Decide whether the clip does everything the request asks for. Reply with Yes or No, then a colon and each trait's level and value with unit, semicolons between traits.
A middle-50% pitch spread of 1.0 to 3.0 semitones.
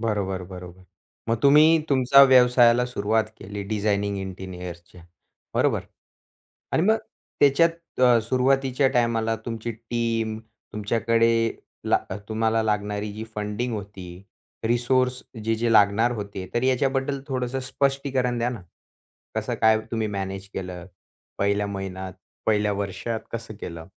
No: average, 3.6 semitones